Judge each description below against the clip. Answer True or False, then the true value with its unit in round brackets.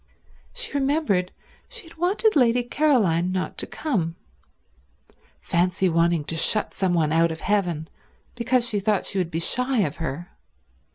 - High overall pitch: True (195 Hz)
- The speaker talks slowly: False (155 wpm)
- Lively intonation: True (7.3 semitones)